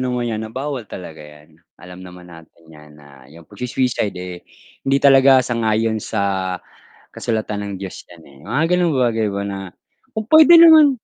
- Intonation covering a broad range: Yes, wide, 6.6 semitones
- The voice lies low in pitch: Yes, low, 110 Hz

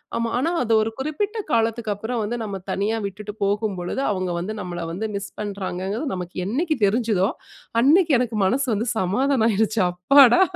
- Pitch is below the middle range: No, high, 220 Hz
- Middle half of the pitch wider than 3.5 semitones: Yes, average, 4.2 semitones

